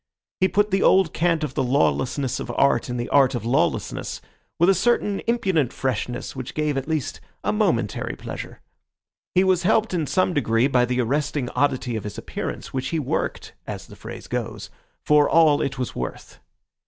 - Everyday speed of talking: Yes, average, 185 wpm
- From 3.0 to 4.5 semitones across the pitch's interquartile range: No, wide, 5.4 semitones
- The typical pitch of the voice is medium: Yes, medium, 145 Hz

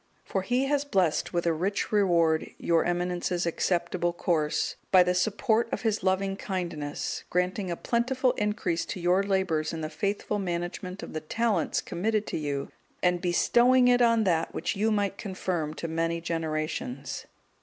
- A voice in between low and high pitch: Yes, medium, 180 Hz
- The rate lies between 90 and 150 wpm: No, average, 165 wpm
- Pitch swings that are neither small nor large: Yes, average, 3.7 semitones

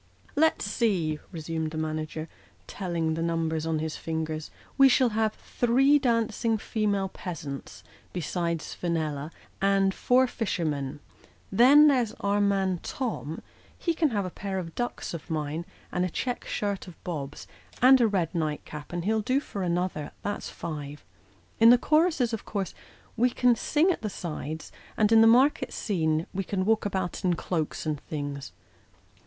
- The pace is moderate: Yes, average, 165 wpm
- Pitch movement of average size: No, wide, 6.1 semitones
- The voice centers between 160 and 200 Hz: Yes, high, 190 Hz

